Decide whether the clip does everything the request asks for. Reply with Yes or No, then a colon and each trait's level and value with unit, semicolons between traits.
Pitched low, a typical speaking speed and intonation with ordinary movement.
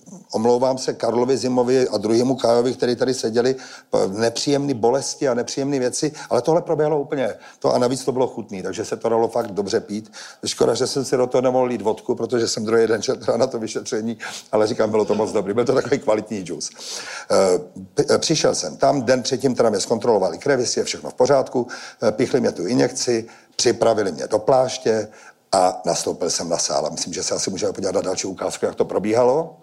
No: low, 125 Hz; fast, 195 wpm; average, 3.2 semitones